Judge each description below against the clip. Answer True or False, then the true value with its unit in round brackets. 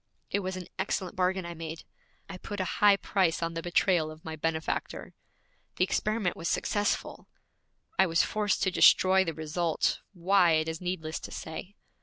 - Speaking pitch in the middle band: True (180 Hz)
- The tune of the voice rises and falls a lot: False (2.7 semitones)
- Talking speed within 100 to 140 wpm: False (175 wpm)